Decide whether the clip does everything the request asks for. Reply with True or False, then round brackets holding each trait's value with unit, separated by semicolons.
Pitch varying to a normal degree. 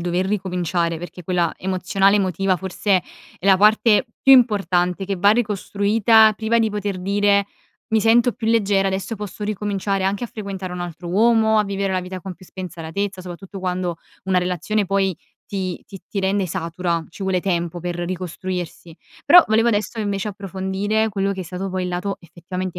False (2.3 semitones)